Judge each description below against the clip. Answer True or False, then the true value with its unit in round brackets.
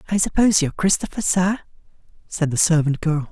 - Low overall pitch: False (170 Hz)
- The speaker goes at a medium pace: True (165 wpm)